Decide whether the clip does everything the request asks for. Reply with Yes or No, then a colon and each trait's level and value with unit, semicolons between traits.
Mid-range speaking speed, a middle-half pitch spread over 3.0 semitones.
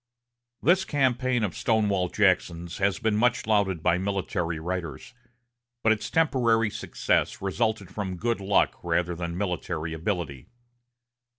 No: slow, 125 wpm; average, 4.4 semitones